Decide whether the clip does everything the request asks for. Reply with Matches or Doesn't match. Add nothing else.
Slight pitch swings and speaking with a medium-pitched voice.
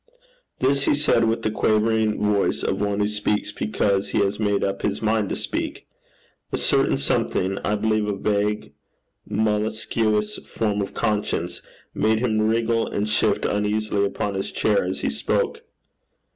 Doesn't match